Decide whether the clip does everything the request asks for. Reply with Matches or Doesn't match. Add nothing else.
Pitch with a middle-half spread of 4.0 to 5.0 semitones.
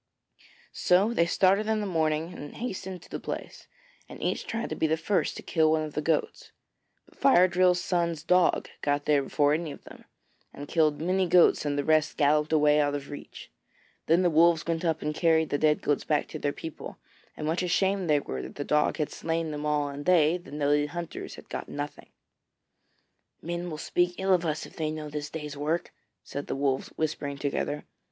Doesn't match